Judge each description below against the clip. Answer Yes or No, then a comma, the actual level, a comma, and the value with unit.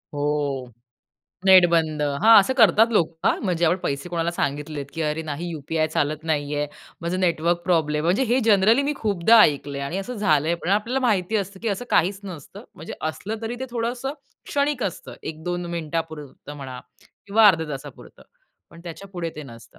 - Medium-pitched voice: Yes, medium, 170 Hz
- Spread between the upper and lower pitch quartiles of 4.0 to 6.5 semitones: Yes, average, 5.1 semitones